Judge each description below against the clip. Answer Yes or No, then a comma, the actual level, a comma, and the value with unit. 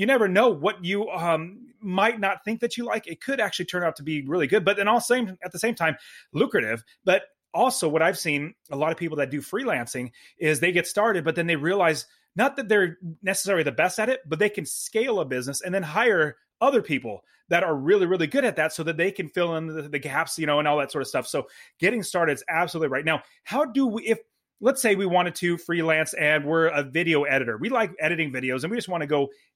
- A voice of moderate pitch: Yes, medium, 175 Hz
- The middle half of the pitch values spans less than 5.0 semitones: No, wide, 5.5 semitones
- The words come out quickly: Yes, fast, 255 wpm